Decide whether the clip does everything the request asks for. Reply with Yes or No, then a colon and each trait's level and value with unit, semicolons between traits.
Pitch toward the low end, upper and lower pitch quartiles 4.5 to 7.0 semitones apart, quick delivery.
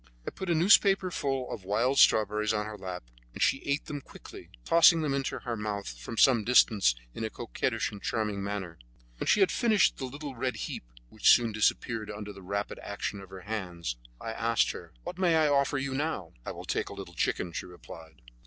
Yes: low, 110 Hz; wide, 5.6 semitones; fast, 210 wpm